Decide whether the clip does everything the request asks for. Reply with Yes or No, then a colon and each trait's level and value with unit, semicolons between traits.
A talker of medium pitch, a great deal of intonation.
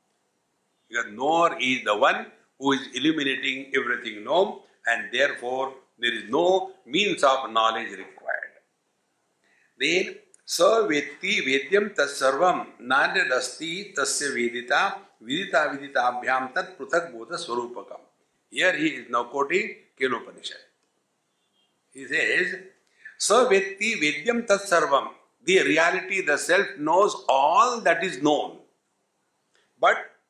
Yes: medium, 145 Hz; wide, 6.5 semitones